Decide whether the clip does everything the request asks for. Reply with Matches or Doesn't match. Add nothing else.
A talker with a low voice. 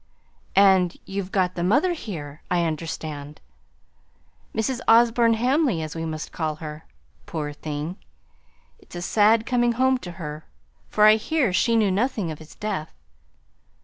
Doesn't match